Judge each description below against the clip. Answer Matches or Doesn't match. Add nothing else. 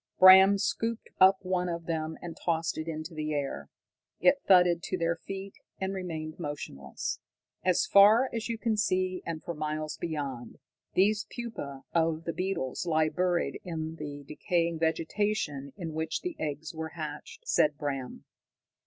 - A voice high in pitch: Doesn't match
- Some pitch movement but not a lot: Matches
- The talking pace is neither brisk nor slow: Matches